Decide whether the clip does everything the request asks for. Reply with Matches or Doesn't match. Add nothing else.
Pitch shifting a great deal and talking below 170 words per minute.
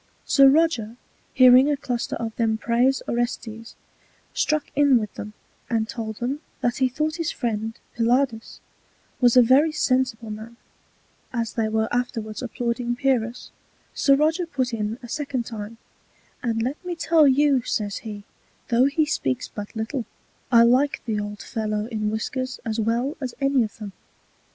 Doesn't match